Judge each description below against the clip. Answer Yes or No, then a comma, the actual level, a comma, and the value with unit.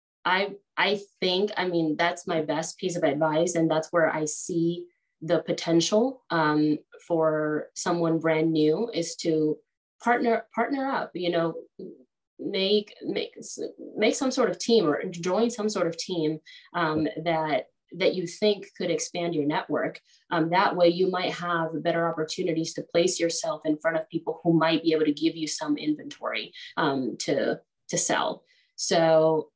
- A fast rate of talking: No, average, 165 wpm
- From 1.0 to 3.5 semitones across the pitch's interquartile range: No, average, 3.9 semitones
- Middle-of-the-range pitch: Yes, medium, 170 Hz